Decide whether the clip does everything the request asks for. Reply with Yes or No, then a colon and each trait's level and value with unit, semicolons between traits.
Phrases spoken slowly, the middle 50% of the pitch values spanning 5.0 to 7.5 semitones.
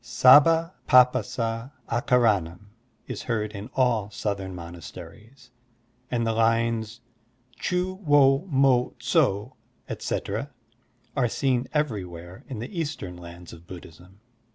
Yes: slow, 115 wpm; average, 5.3 semitones